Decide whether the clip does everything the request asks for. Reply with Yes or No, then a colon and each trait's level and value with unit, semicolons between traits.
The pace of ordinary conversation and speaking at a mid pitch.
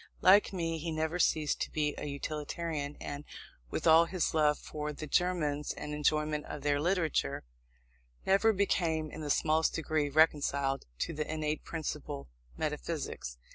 Yes: average, 150 wpm; medium, 155 Hz